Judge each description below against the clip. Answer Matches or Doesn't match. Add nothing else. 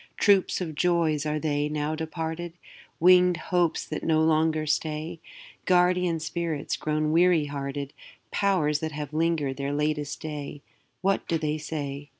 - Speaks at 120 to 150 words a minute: Matches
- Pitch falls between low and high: Matches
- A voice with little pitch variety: Matches